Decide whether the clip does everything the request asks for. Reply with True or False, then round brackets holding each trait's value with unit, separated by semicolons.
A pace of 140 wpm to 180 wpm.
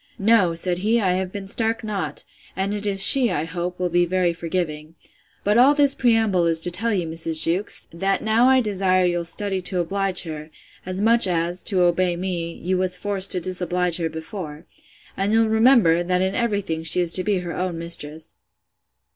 False (200 wpm)